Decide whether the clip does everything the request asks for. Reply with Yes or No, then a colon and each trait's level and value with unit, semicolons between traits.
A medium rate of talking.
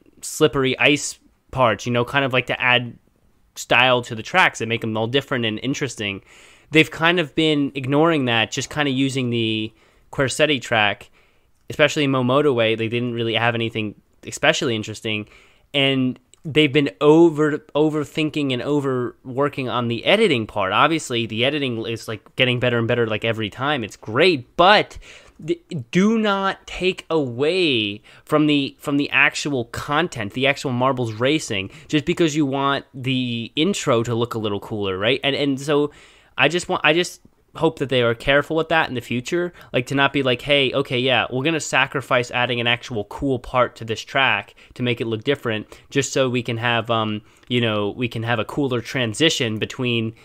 Yes: average, 185 wpm